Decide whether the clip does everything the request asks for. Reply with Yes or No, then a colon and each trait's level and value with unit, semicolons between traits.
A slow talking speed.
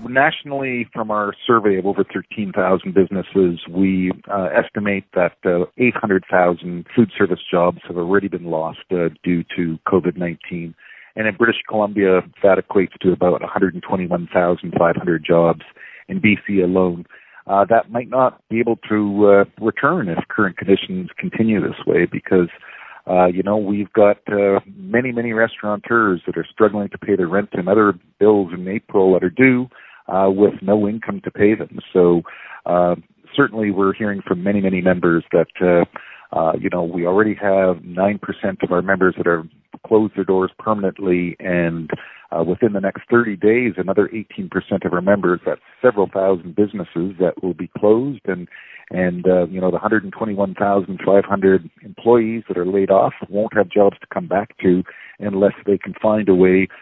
No: average, 165 wpm